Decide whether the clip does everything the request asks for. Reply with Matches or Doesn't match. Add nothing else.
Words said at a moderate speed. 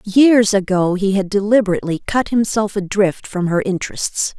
Matches